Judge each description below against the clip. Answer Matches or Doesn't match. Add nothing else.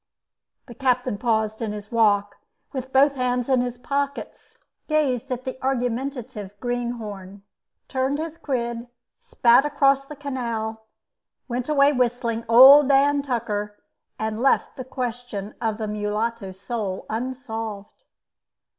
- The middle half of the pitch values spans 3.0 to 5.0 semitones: Matches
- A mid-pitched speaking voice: Doesn't match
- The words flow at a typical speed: Doesn't match